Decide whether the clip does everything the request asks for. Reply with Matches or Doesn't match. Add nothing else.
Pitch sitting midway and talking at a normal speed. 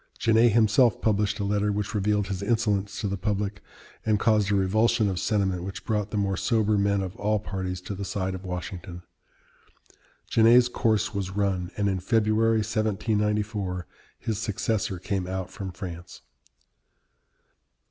Doesn't match